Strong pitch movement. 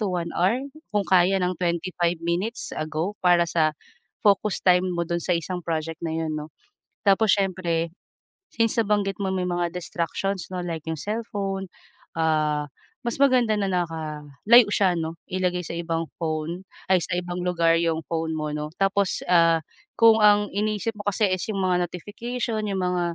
No: average, 3.2 semitones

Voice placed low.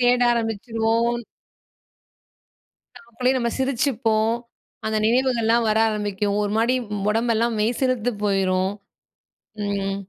No: high, 225 Hz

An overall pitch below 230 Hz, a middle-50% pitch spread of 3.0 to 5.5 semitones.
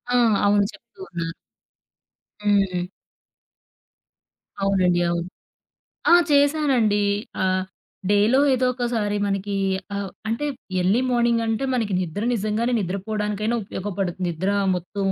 Yes: high, 205 Hz; average, 3.6 semitones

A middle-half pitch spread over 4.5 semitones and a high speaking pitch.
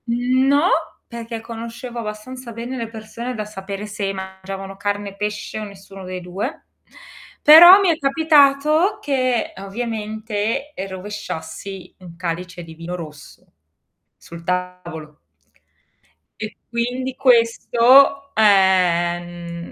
Yes: average, 4.9 semitones; high, 210 Hz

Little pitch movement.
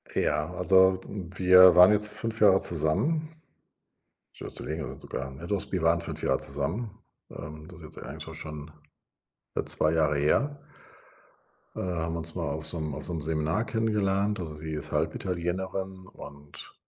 No: average, 3.7 semitones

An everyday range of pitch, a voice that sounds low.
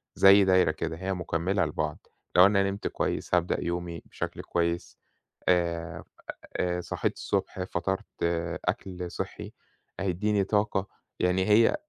No: narrow, 2.2 semitones; very low, 90 Hz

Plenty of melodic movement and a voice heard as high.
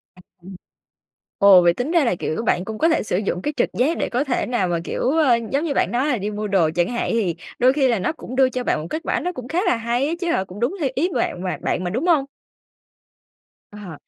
Yes: wide, 6.7 semitones; high, 240 Hz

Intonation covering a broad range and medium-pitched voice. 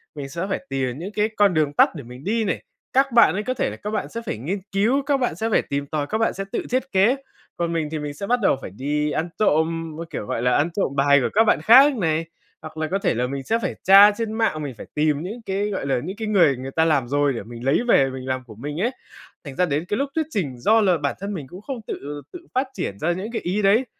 Yes: wide, 6.9 semitones; medium, 170 Hz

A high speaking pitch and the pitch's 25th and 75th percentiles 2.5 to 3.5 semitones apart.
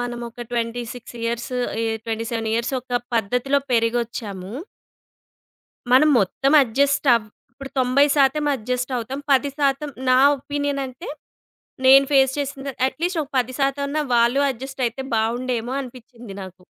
Yes: very high, 250 Hz; average, 2.9 semitones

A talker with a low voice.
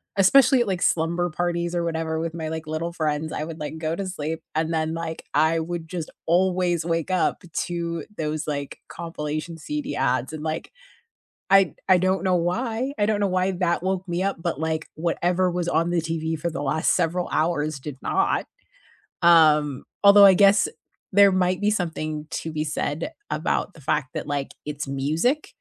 No: medium, 170 Hz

